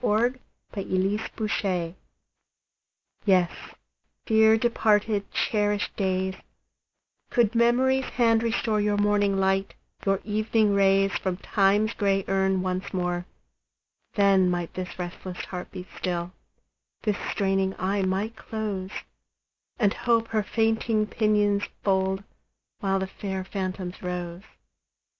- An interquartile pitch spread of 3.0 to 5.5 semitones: No, narrow, 2.4 semitones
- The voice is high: Yes, high, 200 Hz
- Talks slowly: Yes, slow, 110 wpm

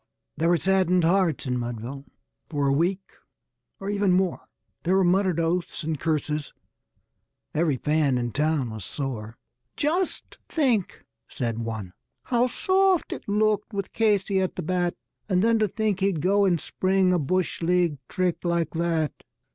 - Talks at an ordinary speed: Yes, average, 160 wpm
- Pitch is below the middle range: No, medium, 175 Hz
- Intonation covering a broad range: No, average, 4.6 semitones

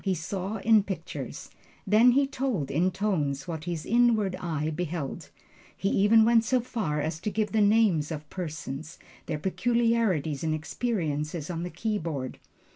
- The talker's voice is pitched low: No, medium, 185 Hz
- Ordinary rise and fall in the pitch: No, wide, 6.0 semitones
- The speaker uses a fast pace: No, average, 155 wpm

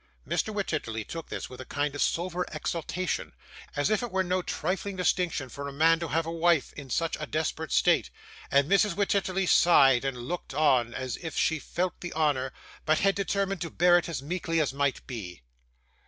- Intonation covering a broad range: No, average, 4.4 semitones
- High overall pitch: No, medium, 165 Hz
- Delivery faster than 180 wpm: Yes, average, 200 wpm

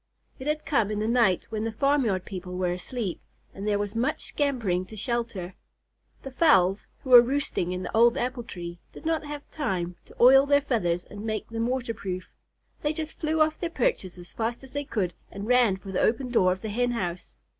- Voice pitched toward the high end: Yes, high, 230 Hz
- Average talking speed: No, fast, 215 wpm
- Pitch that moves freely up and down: Yes, wide, 6.1 semitones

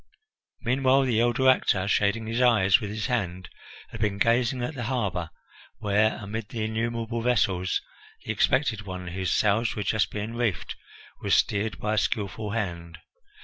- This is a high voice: No, low, 110 Hz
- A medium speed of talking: Yes, average, 160 wpm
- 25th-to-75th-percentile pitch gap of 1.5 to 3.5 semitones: Yes, average, 3.0 semitones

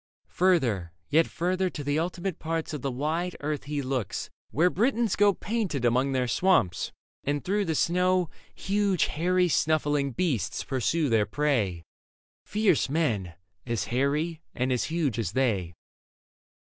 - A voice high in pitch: No, medium, 150 Hz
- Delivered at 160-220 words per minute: No, average, 145 wpm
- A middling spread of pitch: No, wide, 5.9 semitones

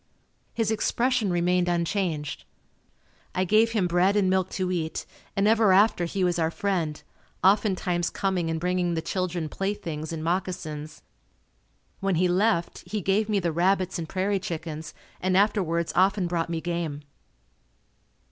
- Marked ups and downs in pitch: No, average, 2.7 semitones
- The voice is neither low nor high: Yes, medium, 180 Hz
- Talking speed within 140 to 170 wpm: Yes, average, 145 wpm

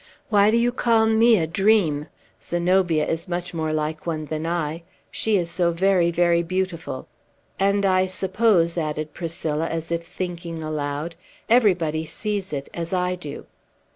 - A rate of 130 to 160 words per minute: Yes, average, 155 wpm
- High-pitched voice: No, medium, 170 Hz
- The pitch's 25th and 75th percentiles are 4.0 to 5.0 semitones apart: No, average, 3.2 semitones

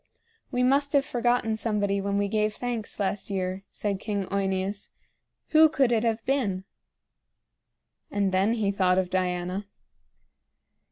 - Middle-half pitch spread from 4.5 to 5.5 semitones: No, average, 3.5 semitones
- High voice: Yes, high, 205 Hz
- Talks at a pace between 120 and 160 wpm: Yes, slow, 135 wpm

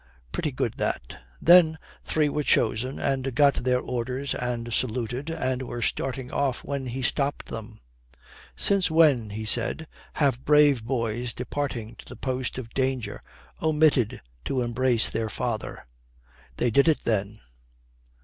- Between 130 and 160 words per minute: Yes, average, 140 wpm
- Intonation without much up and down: No, average, 3.2 semitones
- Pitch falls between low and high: No, low, 130 Hz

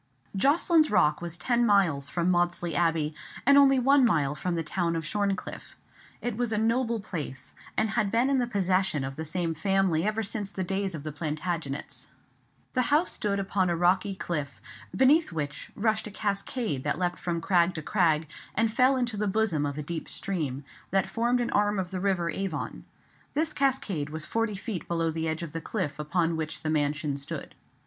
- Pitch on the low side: No, medium, 185 Hz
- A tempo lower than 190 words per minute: No, average, 195 wpm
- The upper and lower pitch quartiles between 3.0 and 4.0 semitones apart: No, wide, 5.4 semitones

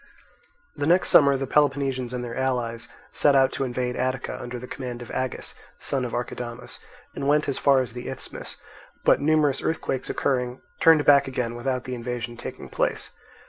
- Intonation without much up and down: Yes, narrow, 2.2 semitones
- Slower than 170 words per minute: No, average, 180 wpm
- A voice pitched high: No, low, 130 Hz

